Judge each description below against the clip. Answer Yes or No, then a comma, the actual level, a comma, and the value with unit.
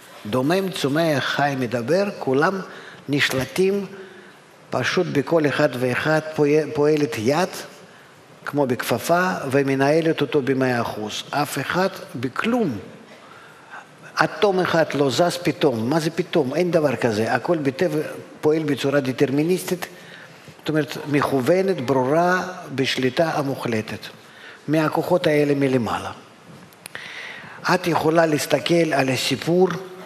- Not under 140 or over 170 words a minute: No, slow, 100 wpm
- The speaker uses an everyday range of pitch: Yes, average, 4.4 semitones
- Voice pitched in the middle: Yes, medium, 150 Hz